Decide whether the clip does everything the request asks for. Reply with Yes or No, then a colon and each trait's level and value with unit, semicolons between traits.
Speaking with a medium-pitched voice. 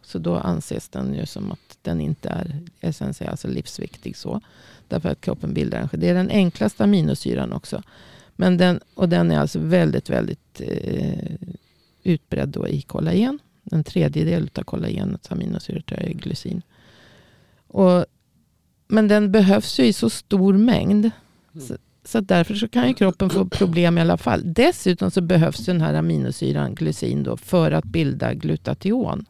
Yes: medium, 180 Hz